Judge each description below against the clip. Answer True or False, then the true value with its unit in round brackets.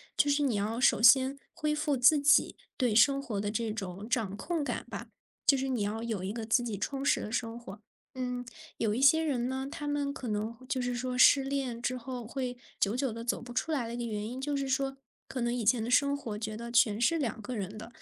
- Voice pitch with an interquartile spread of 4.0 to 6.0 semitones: False (3.6 semitones)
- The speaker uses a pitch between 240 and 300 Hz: True (245 Hz)